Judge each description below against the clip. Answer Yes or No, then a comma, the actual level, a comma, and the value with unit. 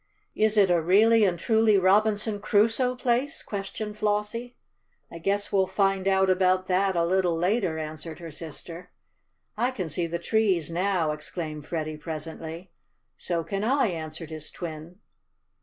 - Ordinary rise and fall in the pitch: Yes, average, 4.2 semitones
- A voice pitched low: No, medium, 185 Hz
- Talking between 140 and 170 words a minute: Yes, average, 150 wpm